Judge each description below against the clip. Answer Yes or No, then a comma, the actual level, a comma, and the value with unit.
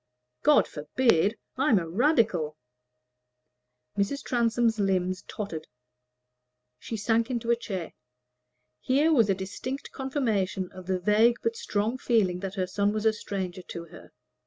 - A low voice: No, high, 210 Hz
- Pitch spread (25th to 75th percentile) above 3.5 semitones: Yes, average, 4.3 semitones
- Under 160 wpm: Yes, slow, 135 wpm